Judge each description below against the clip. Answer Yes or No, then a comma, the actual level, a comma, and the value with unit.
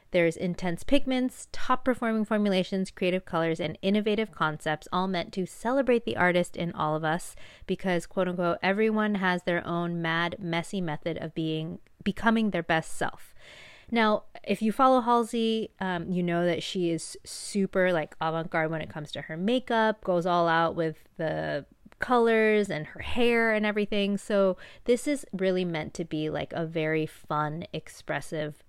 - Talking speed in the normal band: Yes, average, 165 wpm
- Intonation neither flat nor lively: Yes, average, 4.7 semitones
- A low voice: No, medium, 180 Hz